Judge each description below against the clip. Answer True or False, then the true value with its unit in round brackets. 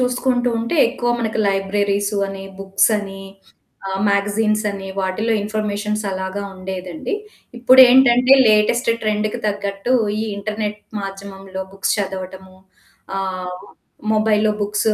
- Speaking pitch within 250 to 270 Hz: False (205 Hz)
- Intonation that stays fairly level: True (2.0 semitones)